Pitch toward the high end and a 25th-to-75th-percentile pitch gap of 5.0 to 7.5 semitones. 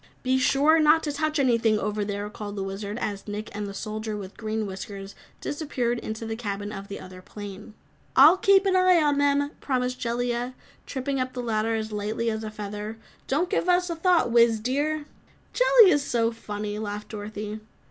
Yes: high, 225 Hz; average, 5.3 semitones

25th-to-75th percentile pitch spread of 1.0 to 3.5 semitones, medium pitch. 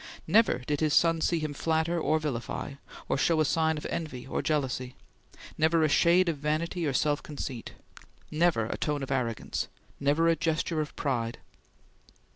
Yes: average, 2.9 semitones; medium, 155 Hz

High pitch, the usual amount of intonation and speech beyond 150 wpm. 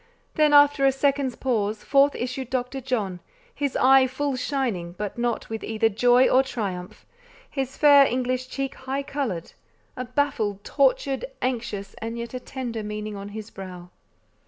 Yes: very high, 250 Hz; average, 4.1 semitones; average, 160 wpm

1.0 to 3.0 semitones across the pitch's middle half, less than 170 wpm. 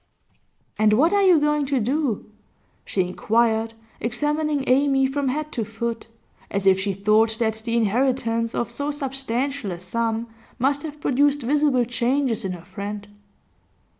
No: average, 4.4 semitones; average, 150 wpm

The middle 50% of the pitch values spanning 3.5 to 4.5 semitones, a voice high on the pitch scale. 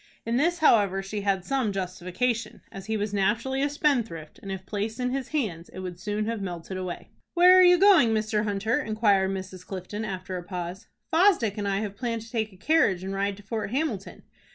Yes: average, 3.9 semitones; high, 210 Hz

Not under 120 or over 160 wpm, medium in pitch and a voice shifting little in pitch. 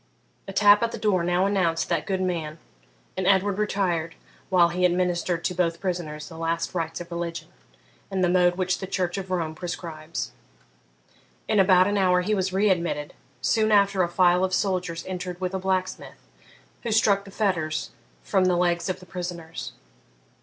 No: average, 180 wpm; medium, 180 Hz; narrow, 1.9 semitones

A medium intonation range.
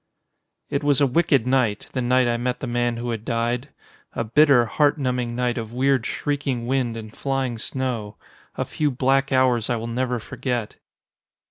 No: narrow, 2.3 semitones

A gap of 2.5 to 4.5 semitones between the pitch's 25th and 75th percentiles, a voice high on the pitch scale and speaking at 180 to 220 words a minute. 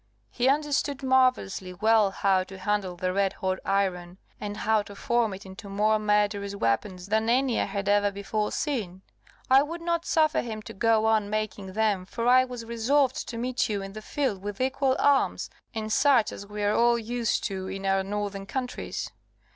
Yes: average, 3.8 semitones; high, 215 Hz; average, 190 wpm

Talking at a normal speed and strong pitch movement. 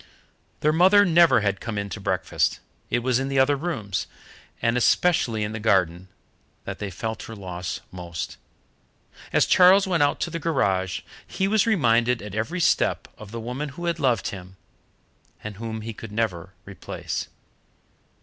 Yes: average, 170 wpm; wide, 7.2 semitones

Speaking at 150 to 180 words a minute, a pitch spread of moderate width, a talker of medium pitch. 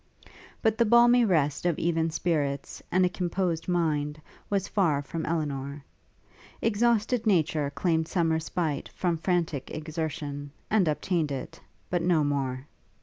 No: slow, 135 wpm; average, 3.8 semitones; medium, 165 Hz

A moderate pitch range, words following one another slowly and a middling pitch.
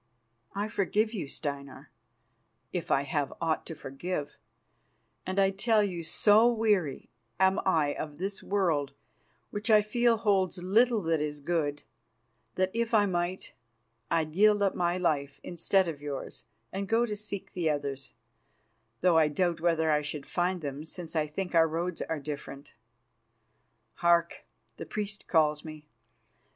No: average, 4.8 semitones; average, 155 wpm; medium, 175 Hz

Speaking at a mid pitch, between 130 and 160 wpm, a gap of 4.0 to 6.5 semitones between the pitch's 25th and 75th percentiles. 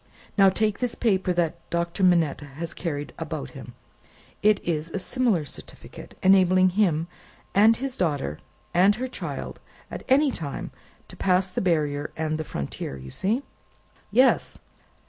Yes: medium, 180 Hz; average, 145 wpm; average, 4.8 semitones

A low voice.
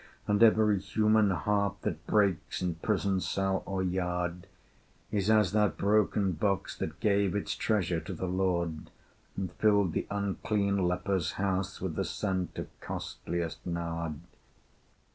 Yes: very low, 95 Hz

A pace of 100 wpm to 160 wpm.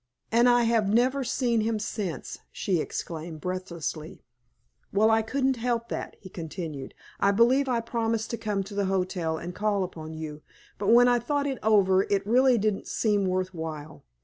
No: average, 175 wpm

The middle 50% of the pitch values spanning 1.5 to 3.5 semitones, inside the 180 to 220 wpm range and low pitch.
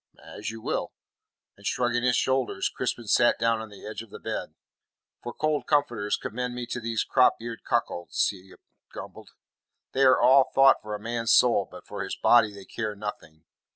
Yes: average, 3.0 semitones; average, 185 wpm; low, 115 Hz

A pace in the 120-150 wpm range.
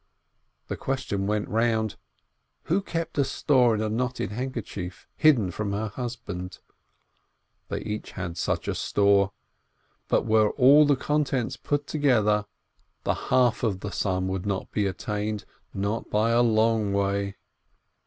Yes: average, 145 wpm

